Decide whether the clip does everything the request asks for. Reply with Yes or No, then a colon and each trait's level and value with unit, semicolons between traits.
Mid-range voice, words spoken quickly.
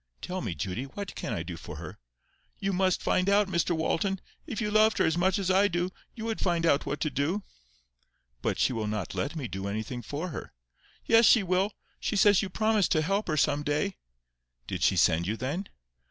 Yes: medium, 180 Hz; fast, 215 wpm